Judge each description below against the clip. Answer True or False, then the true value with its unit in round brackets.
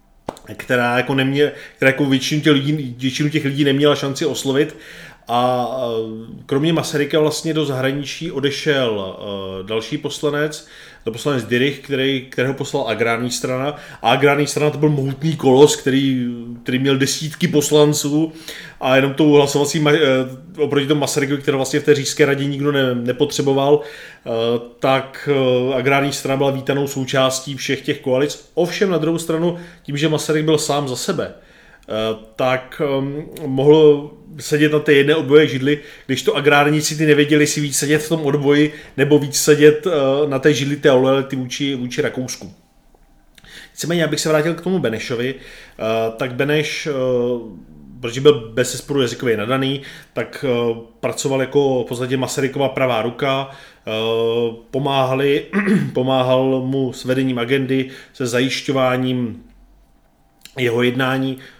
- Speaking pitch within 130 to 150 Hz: True (140 Hz)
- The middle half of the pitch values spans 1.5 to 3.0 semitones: True (2.5 semitones)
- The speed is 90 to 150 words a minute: True (145 wpm)